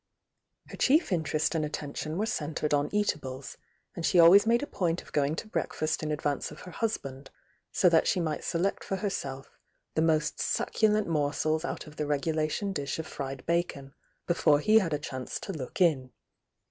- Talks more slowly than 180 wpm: No, average, 185 wpm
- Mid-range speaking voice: Yes, medium, 155 Hz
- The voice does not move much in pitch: No, average, 3.9 semitones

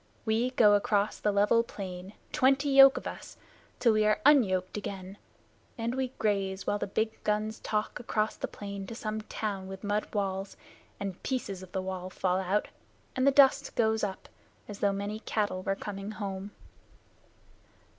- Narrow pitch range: Yes, narrow, 2.3 semitones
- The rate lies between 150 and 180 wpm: Yes, average, 170 wpm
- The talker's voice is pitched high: Yes, high, 205 Hz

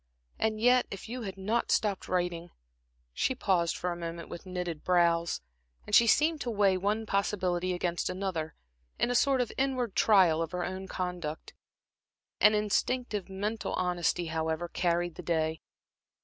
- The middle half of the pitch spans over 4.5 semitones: No, average, 3.6 semitones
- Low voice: No, medium, 185 Hz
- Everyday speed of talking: Yes, average, 160 wpm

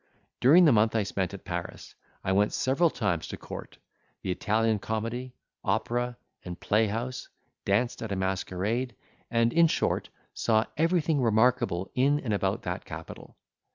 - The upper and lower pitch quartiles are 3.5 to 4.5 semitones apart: Yes, average, 4.1 semitones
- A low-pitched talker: Yes, low, 115 Hz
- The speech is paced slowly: No, average, 150 wpm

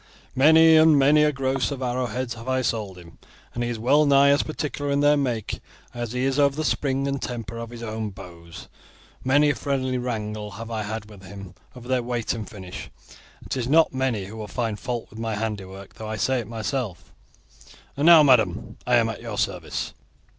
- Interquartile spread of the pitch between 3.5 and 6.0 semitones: Yes, average, 3.9 semitones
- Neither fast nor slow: No, fast, 210 wpm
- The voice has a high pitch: No, low, 120 Hz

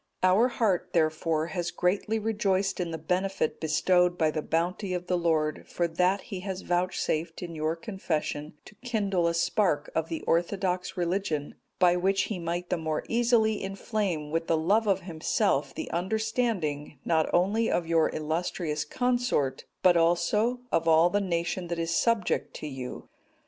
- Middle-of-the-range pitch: Yes, medium, 175 Hz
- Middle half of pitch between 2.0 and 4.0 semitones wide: Yes, average, 3.4 semitones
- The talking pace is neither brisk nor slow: Yes, average, 165 wpm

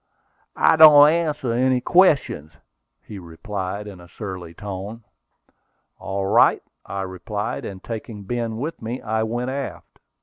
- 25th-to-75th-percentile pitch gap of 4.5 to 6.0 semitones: Yes, average, 5.0 semitones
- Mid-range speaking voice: No, low, 110 Hz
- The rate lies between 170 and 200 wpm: No, slow, 135 wpm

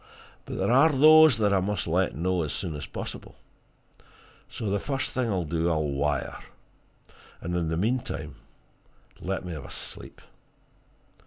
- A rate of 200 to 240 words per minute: No, average, 160 wpm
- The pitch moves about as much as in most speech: No, wide, 6.5 semitones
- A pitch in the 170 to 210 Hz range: No, very low, 95 Hz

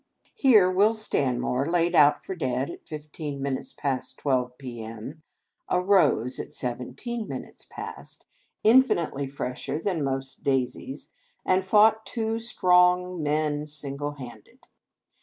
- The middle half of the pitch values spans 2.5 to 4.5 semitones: No, wide, 5.5 semitones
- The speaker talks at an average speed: No, slow, 120 wpm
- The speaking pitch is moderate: Yes, medium, 150 Hz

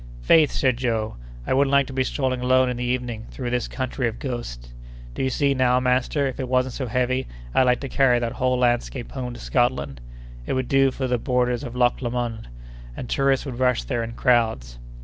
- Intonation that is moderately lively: No, narrow, 1.5 semitones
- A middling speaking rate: No, fast, 215 wpm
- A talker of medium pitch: No, low, 125 Hz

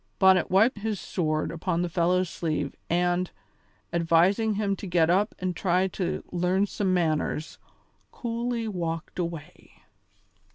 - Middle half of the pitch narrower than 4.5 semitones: Yes, average, 2.8 semitones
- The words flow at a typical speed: No, slow, 130 wpm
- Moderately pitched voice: Yes, medium, 180 Hz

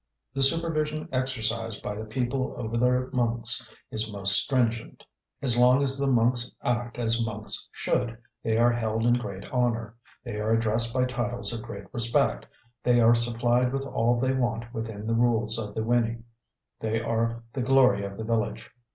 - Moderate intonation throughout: No, narrow, 1.8 semitones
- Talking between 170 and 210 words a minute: Yes, average, 175 wpm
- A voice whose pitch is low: Yes, low, 115 Hz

